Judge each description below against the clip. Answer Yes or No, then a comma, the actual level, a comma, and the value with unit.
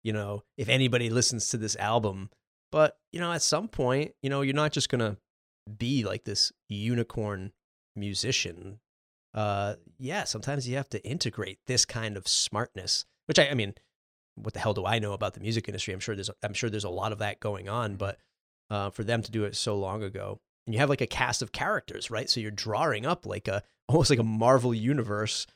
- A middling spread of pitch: Yes, average, 3.6 semitones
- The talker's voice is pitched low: Yes, low, 110 Hz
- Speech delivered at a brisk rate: Yes, fast, 220 wpm